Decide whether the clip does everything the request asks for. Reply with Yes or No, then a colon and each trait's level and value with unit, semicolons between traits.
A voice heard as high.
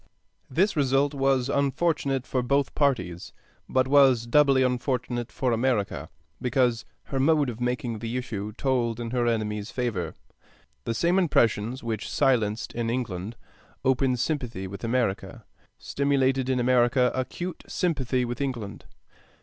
No: low, 125 Hz